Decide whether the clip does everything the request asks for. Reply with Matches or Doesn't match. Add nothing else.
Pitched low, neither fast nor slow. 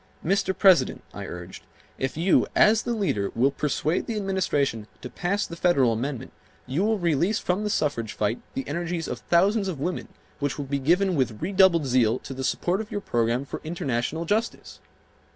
Doesn't match